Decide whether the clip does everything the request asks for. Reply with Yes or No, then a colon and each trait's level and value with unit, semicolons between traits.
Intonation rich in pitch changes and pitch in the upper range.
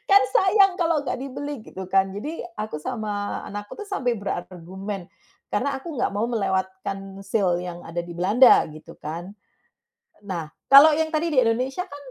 Yes: wide, 6.6 semitones; high, 205 Hz